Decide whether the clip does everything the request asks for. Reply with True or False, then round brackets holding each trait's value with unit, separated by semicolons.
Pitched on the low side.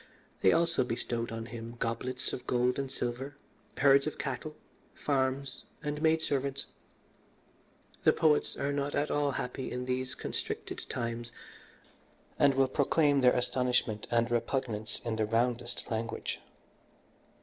True (130 Hz)